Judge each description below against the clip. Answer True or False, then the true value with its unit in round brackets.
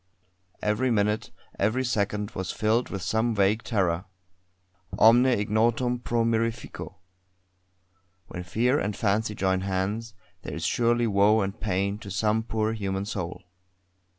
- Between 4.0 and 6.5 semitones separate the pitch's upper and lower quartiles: False (2.6 semitones)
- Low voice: True (110 Hz)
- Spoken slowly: True (130 wpm)